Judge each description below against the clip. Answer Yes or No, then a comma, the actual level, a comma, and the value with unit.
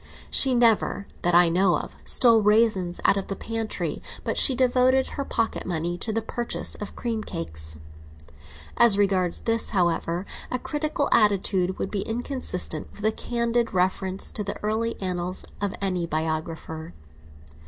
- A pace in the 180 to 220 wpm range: No, average, 155 wpm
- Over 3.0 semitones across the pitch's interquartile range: Yes, average, 4.5 semitones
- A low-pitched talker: No, high, 200 Hz